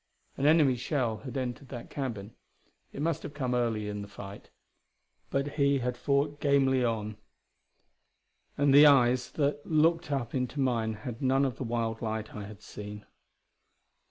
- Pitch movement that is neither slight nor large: Yes, average, 3.9 semitones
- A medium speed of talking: Yes, average, 160 wpm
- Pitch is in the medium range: No, low, 130 Hz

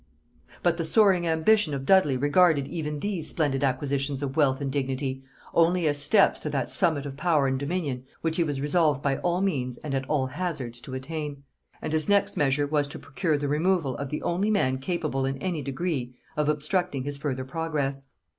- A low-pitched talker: No, medium, 145 Hz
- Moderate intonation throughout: Yes, average, 3.7 semitones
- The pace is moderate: Yes, average, 195 wpm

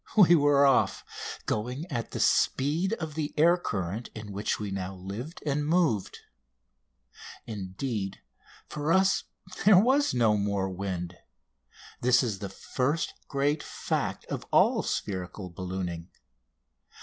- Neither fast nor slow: No, slow, 130 wpm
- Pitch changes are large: Yes, wide, 7.7 semitones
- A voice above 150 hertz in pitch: No, low, 120 Hz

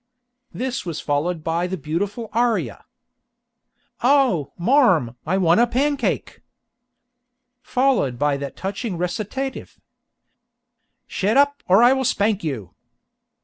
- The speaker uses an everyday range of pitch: No, wide, 7.3 semitones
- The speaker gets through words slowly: Yes, slow, 110 wpm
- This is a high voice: Yes, high, 195 Hz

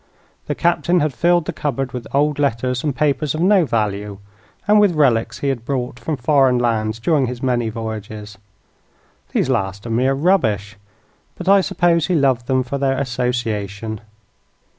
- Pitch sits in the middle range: No, low, 130 Hz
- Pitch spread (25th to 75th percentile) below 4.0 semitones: No, average, 4.9 semitones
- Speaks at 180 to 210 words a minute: No, average, 165 wpm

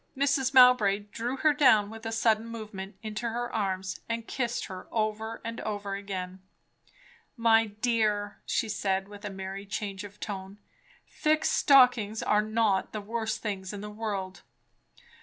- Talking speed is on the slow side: No, average, 155 wpm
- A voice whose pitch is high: Yes, high, 215 Hz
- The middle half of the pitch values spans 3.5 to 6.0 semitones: No, narrow, 2.5 semitones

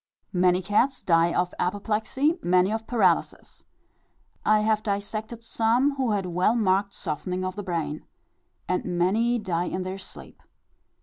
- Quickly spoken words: No, average, 140 wpm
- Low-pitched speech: No, high, 200 Hz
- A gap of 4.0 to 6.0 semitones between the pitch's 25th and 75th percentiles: No, average, 3.6 semitones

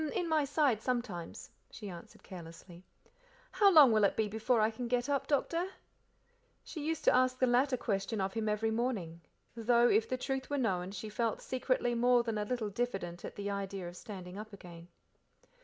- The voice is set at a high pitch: Yes, high, 225 Hz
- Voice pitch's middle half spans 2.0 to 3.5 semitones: No, average, 4.4 semitones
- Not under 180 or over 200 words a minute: Yes, average, 195 wpm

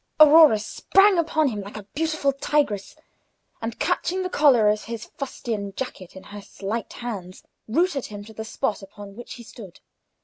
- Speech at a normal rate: Yes, average, 170 wpm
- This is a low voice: No, high, 230 Hz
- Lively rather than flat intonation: Yes, wide, 6.3 semitones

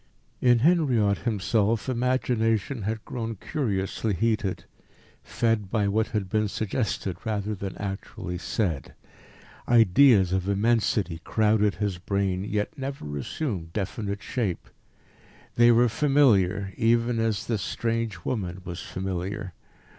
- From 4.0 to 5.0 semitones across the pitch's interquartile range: No, average, 3.2 semitones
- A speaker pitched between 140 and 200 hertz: No, low, 105 Hz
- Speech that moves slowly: Yes, slow, 115 wpm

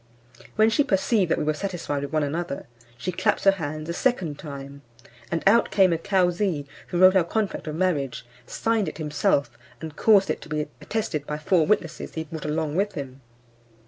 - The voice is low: No, medium, 165 Hz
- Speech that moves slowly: No, average, 195 wpm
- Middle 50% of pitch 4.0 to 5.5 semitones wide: Yes, average, 4.4 semitones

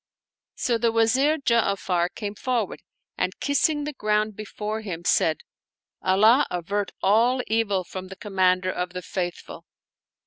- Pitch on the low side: No, high, 210 Hz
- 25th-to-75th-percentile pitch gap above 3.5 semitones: Yes, average, 3.9 semitones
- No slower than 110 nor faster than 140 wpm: Yes, slow, 135 wpm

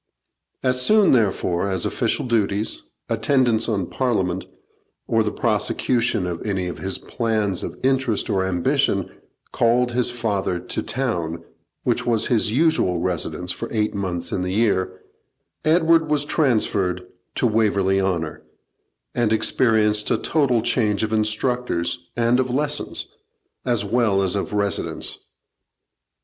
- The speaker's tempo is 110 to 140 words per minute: Yes, slow, 135 wpm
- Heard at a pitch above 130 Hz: No, low, 110 Hz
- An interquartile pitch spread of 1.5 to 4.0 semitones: No, average, 4.5 semitones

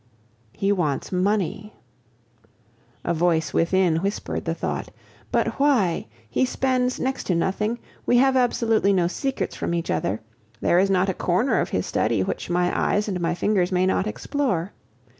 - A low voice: No, high, 190 Hz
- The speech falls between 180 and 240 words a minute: No, average, 160 wpm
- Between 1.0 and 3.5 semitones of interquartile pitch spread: No, average, 4.7 semitones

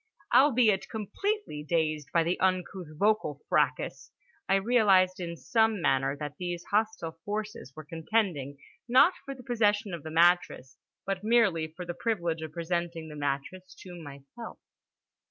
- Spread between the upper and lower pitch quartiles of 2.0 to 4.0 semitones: No, average, 5.2 semitones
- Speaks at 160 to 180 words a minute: No, average, 145 wpm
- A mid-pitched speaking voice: Yes, medium, 180 Hz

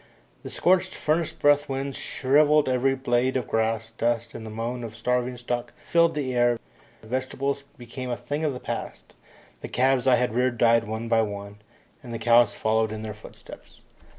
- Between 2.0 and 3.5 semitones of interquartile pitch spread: Yes, average, 2.8 semitones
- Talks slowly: No, average, 180 wpm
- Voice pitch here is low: Yes, low, 120 Hz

